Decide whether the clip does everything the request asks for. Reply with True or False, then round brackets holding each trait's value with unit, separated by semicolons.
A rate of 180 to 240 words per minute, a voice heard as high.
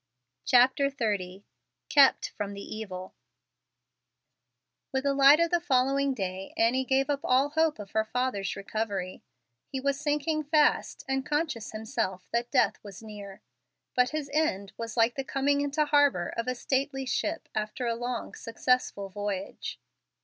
False (150 wpm; 250 Hz)